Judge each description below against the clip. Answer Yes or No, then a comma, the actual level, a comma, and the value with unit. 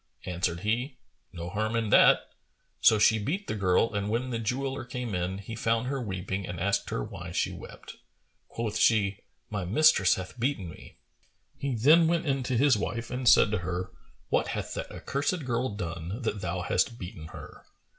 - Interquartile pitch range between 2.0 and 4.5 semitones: No, average, 5.2 semitones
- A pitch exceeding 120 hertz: No, low, 110 Hz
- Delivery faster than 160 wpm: Yes, average, 185 wpm